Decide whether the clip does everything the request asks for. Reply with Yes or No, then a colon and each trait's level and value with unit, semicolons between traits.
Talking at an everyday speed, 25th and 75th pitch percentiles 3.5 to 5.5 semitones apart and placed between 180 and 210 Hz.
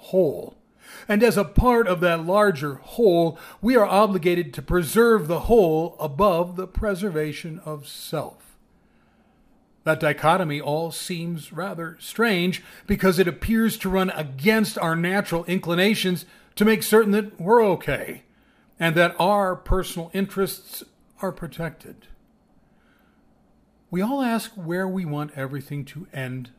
No: slow, 130 wpm; average, 4.1 semitones; medium, 185 Hz